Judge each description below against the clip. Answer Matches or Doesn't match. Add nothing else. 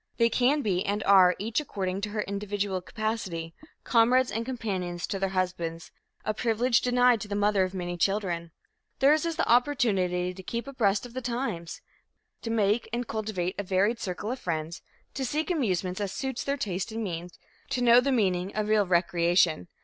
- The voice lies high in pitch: Matches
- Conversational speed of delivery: Matches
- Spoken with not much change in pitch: Doesn't match